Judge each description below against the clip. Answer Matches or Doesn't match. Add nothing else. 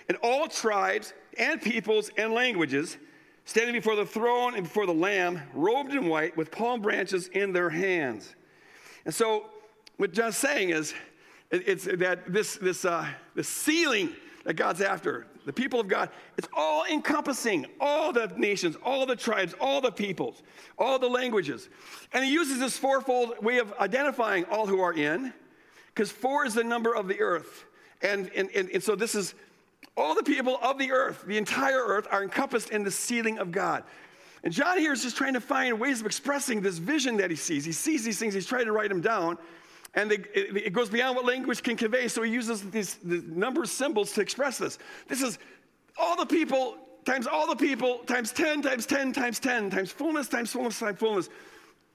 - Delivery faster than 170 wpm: Matches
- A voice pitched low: Doesn't match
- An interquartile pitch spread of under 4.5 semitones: Doesn't match